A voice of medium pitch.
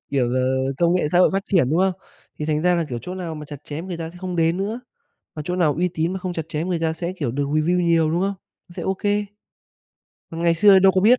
Yes: medium, 170 Hz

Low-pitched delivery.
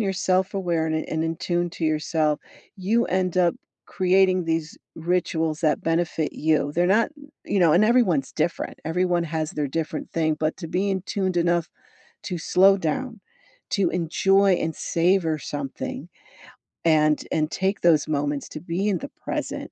No: medium, 170 Hz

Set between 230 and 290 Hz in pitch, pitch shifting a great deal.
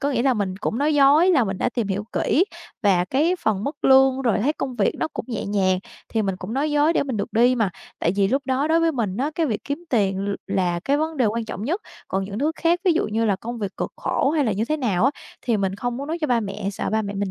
Yes: high, 235 Hz; wide, 6.1 semitones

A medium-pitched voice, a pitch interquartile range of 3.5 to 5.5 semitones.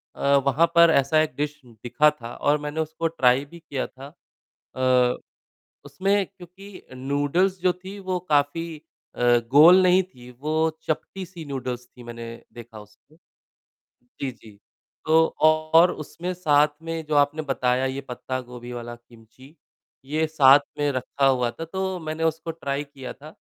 Yes: medium, 145 Hz; average, 4.3 semitones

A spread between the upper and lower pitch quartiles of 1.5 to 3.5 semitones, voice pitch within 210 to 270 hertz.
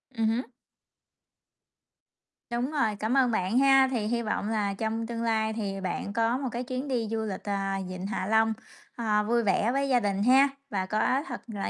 Yes: average, 2.9 semitones; high, 225 Hz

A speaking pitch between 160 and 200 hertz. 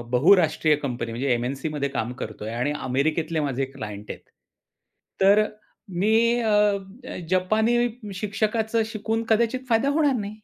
Yes: medium, 185 Hz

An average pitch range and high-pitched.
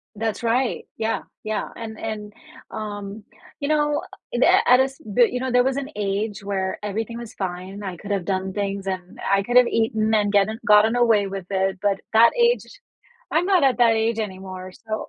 Yes: average, 3.1 semitones; high, 215 Hz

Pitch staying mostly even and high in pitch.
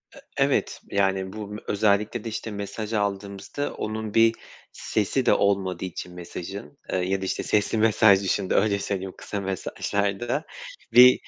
No: narrow, 2.1 semitones; low, 100 Hz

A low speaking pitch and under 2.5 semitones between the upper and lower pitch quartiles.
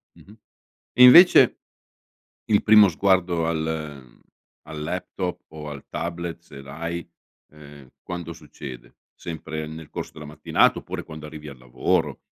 No: very low, 80 Hz; average, 2.8 semitones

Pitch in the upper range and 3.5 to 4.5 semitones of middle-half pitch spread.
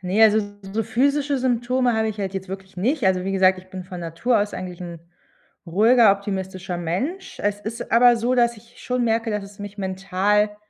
Yes: high, 210 Hz; average, 3.9 semitones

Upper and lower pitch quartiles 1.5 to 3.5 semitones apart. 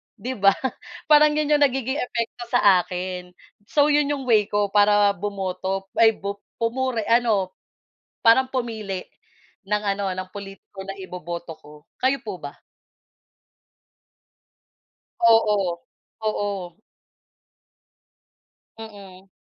No: average, 4.0 semitones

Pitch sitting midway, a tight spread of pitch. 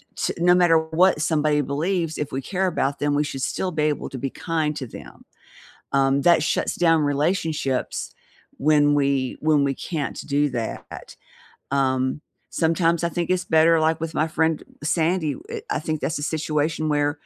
Yes: medium, 155 Hz; narrow, 2.3 semitones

